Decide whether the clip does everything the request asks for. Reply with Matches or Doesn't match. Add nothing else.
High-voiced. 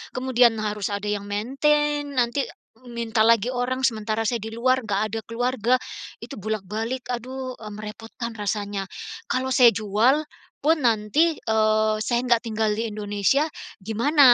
Matches